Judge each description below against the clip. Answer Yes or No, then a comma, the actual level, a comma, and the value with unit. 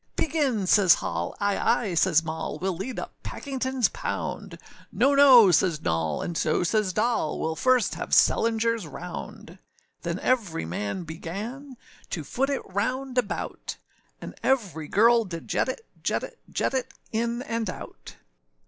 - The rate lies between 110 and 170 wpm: Yes, average, 155 wpm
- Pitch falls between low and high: No, high, 215 Hz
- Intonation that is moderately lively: No, wide, 7.2 semitones